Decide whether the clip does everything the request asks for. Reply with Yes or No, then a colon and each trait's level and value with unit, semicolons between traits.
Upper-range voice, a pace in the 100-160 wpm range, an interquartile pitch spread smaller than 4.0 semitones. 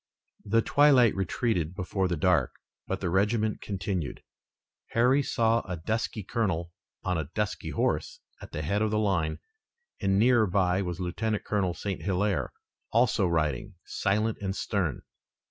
No: low, 100 Hz; average, 145 wpm; average, 3.5 semitones